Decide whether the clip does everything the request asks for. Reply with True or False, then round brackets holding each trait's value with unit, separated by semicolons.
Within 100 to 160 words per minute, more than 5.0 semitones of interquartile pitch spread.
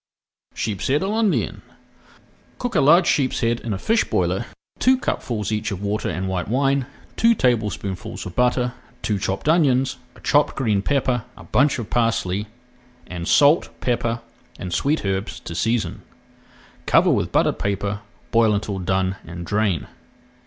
True (155 wpm; 5.5 semitones)